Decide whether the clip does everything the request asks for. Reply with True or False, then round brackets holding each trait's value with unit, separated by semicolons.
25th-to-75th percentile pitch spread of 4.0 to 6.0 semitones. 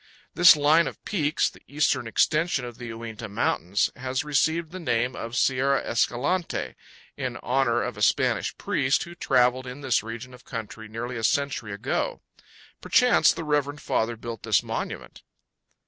True (4.3 semitones)